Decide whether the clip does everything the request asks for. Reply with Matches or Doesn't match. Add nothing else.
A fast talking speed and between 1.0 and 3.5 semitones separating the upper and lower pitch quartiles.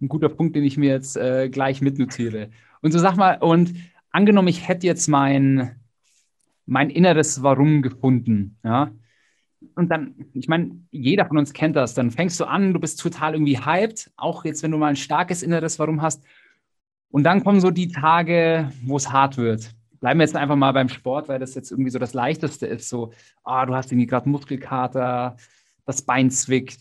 Doesn't match